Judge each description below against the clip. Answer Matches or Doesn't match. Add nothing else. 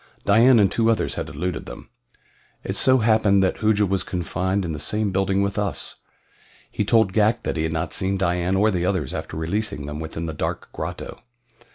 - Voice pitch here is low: Matches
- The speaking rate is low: Doesn't match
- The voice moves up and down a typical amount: Matches